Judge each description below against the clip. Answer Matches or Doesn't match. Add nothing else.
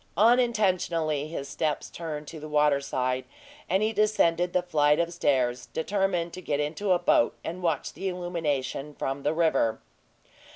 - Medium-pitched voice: Matches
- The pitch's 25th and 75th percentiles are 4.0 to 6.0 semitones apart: Doesn't match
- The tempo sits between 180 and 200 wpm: Doesn't match